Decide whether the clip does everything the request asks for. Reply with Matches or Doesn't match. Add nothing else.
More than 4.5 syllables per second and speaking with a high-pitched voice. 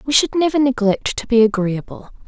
Matches